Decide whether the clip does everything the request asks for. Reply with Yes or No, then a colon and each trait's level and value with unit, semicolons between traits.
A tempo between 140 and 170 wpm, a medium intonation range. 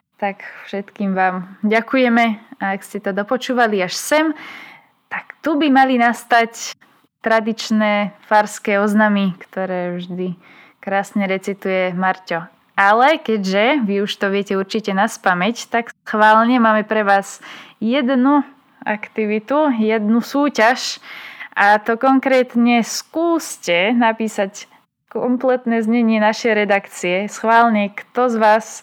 No: average, 115 wpm; average, 3.5 semitones